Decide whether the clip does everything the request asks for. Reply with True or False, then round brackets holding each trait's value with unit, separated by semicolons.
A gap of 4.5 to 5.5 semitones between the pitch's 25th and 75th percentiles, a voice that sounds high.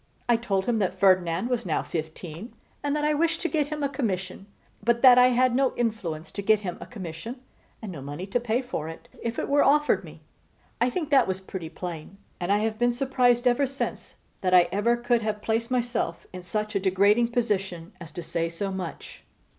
True (5.2 semitones; 215 Hz)